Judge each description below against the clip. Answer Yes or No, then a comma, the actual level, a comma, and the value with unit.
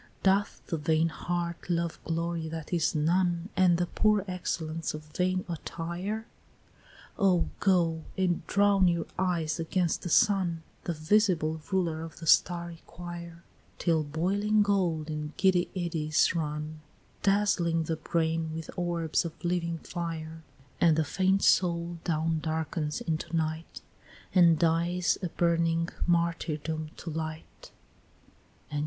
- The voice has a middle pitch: Yes, medium, 170 Hz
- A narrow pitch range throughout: Yes, narrow, 2.0 semitones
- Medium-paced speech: No, slow, 130 wpm